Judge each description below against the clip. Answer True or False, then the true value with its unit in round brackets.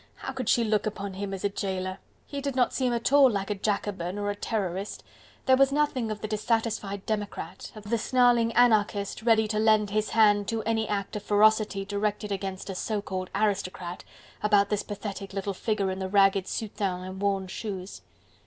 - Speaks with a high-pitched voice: True (205 Hz)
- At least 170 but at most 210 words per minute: True (195 wpm)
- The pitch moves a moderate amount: False (2.1 semitones)